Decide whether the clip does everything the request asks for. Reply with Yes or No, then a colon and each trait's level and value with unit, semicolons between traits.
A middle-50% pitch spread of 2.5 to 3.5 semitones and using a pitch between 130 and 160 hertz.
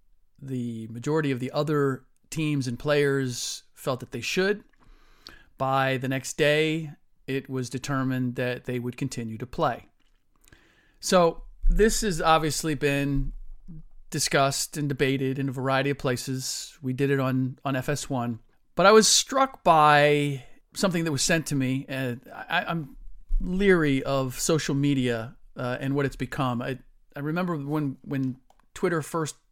Yes: average, 3.1 semitones; medium, 140 Hz